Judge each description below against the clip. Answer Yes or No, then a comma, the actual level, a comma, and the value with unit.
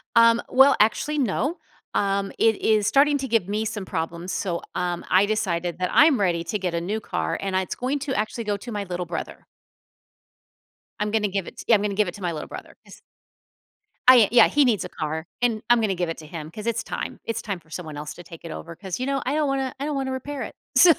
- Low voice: No, high, 205 Hz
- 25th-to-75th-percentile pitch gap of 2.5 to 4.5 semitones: No, wide, 5.5 semitones